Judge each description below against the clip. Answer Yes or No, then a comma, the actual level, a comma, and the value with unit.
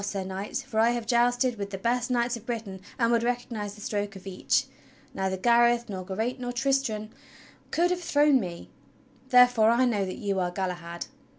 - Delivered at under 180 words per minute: No, average, 190 wpm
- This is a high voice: Yes, high, 230 Hz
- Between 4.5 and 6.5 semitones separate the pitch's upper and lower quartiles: No, average, 3.9 semitones